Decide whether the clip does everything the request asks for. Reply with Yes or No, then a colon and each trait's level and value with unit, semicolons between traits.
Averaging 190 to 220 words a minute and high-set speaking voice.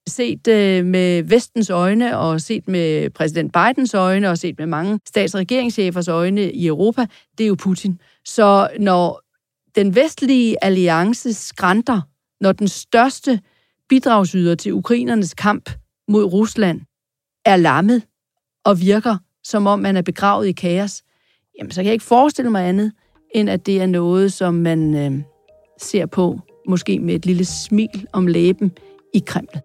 No: average, 155 wpm; high, 195 Hz